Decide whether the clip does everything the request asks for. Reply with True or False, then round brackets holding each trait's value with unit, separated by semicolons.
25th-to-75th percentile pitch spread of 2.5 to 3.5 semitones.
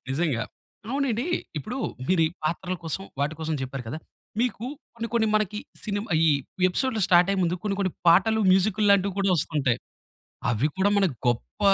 False (5.1 semitones)